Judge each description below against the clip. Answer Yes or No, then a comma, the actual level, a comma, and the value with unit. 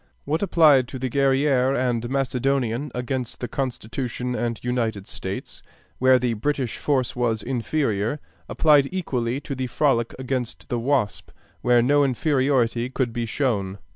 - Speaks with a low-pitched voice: Yes, low, 125 Hz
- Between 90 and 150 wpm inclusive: Yes, average, 140 wpm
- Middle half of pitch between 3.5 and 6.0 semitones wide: No, average, 2.7 semitones